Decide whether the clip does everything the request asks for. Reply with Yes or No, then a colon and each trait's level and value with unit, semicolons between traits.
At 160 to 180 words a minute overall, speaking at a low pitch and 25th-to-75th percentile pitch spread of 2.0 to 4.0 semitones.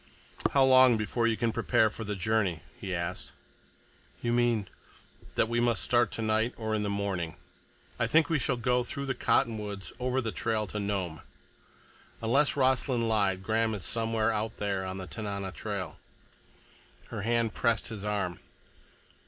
Yes: average, 165 wpm; low, 110 Hz; average, 2.9 semitones